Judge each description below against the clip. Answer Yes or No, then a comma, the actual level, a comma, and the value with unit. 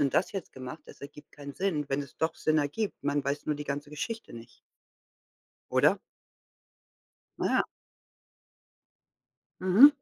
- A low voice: No, medium, 145 Hz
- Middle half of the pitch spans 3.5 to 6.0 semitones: Yes, average, 4.2 semitones